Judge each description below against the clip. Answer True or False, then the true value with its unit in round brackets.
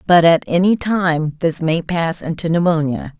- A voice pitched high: False (165 Hz)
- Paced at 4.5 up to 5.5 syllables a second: False (4.3 syllables/s)